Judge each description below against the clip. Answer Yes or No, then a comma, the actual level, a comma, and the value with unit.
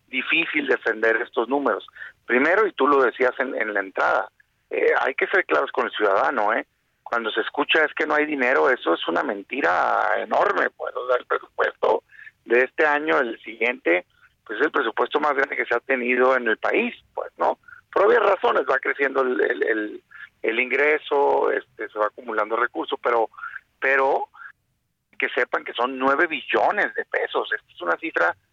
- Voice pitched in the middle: Yes, medium, 175 Hz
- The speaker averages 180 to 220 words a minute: Yes, average, 185 wpm